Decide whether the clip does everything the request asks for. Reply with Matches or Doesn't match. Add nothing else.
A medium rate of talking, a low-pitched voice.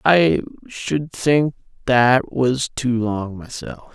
Doesn't match